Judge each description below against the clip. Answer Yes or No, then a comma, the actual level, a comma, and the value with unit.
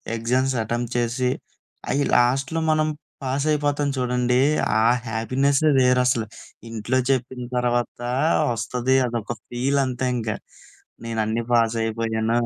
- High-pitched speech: No, low, 125 Hz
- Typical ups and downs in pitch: No, narrow, 2.2 semitones